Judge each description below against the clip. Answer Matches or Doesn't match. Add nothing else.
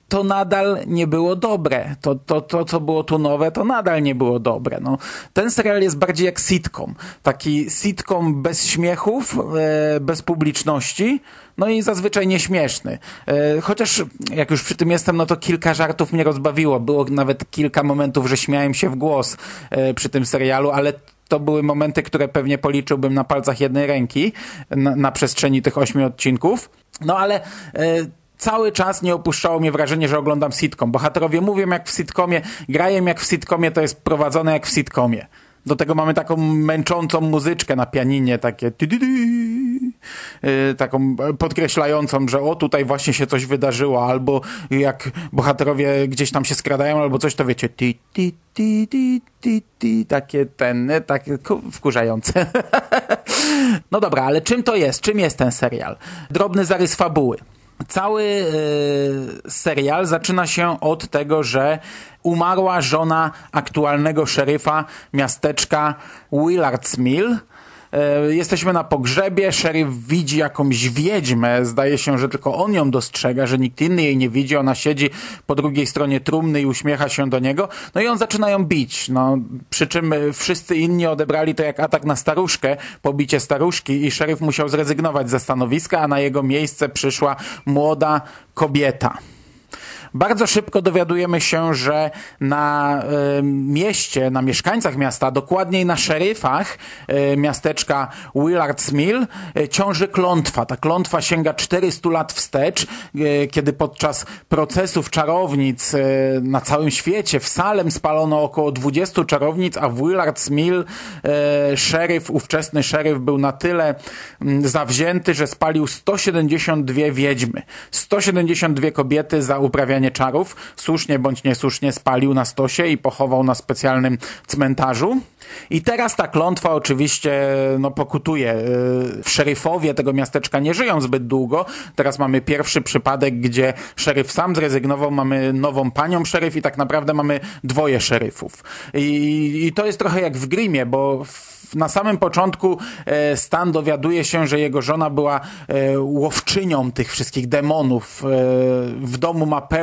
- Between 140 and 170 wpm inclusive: Matches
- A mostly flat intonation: Doesn't match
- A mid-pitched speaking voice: Matches